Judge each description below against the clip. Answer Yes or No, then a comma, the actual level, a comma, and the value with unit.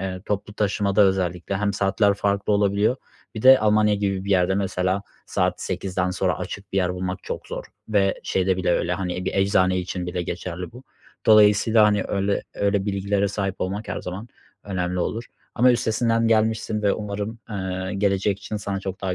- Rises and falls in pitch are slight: Yes, narrow, 2.0 semitones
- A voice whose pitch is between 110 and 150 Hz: No, low, 100 Hz